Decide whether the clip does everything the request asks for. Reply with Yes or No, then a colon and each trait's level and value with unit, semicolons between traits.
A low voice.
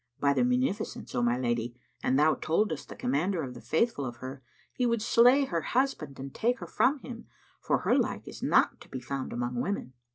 No: medium, 155 Hz